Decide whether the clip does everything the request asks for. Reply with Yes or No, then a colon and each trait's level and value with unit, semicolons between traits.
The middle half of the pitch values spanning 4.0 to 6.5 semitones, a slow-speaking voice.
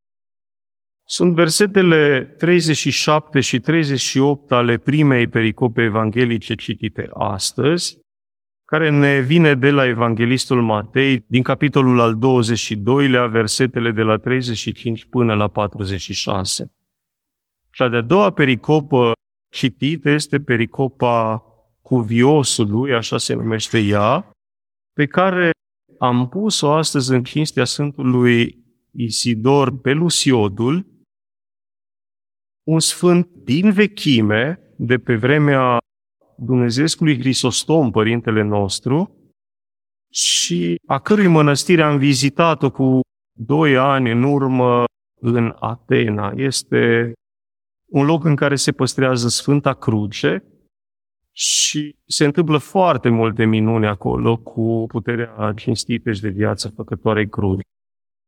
Yes: average, 4.5 semitones; slow, 100 wpm